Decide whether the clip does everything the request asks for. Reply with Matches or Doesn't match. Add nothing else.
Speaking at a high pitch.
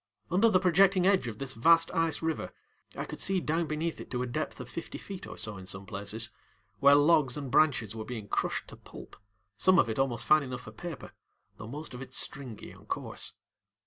Doesn't match